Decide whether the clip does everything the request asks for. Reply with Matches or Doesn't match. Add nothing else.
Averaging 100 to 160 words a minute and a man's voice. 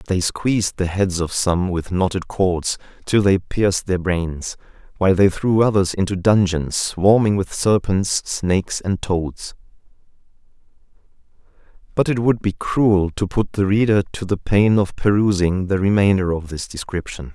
Matches